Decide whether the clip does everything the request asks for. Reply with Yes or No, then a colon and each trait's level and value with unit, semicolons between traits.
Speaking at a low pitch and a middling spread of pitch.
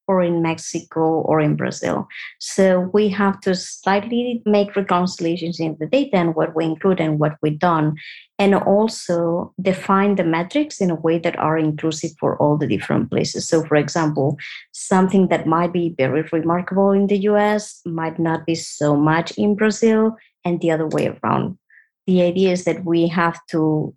No: medium, 170 Hz; average, 3.4 semitones